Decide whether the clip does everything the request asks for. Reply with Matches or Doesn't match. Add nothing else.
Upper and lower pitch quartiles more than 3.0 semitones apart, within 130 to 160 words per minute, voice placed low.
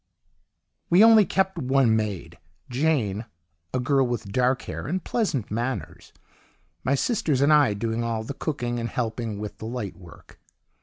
Matches